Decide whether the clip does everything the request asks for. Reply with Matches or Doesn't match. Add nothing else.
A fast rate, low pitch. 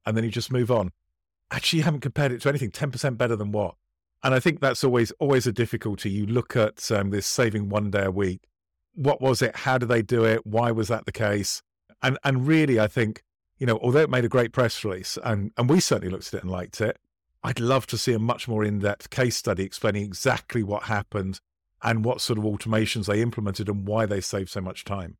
Matches